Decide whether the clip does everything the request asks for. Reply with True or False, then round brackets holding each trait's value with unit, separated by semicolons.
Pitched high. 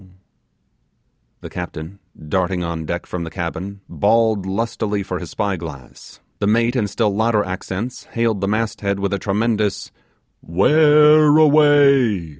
False (100 Hz)